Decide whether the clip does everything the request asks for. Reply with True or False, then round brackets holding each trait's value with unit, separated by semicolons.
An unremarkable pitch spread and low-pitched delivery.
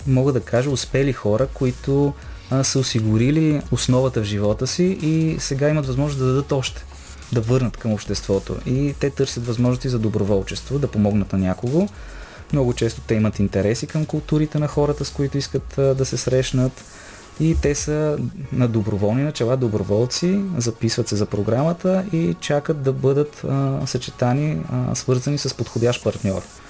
True (4.1 semitones; 130 Hz)